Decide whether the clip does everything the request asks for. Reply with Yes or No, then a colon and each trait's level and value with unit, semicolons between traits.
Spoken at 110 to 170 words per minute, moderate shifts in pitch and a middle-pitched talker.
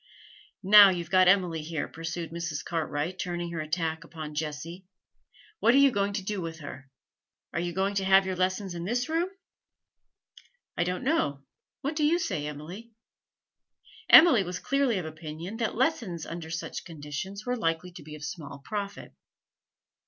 Yes: average, 165 wpm; average, 3.9 semitones; medium, 175 Hz